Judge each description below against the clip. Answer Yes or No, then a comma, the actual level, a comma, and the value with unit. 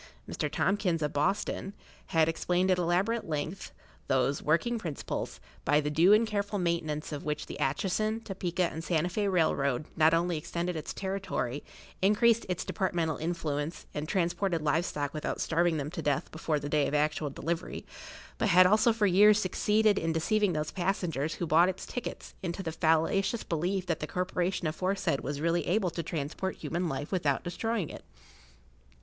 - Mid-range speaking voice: Yes, medium, 170 Hz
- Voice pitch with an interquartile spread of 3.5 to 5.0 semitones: Yes, average, 3.8 semitones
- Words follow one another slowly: No, average, 170 wpm